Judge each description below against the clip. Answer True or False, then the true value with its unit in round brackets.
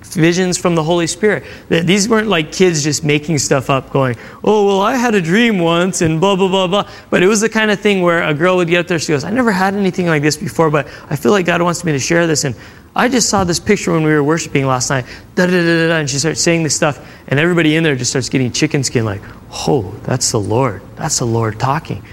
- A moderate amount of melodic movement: True (4.8 semitones)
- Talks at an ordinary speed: False (260 wpm)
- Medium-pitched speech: True (165 Hz)